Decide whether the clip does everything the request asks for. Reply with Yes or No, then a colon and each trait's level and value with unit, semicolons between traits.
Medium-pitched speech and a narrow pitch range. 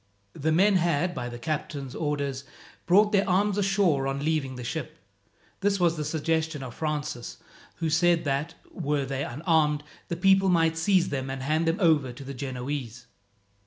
No: medium, 155 Hz; average, 3.9 semitones